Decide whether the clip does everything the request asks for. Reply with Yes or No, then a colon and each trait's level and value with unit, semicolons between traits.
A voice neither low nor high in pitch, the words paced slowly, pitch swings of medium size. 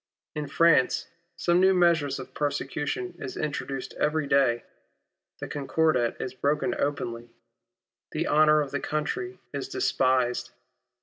Yes: medium, 145 Hz; slow, 125 wpm; average, 3.3 semitones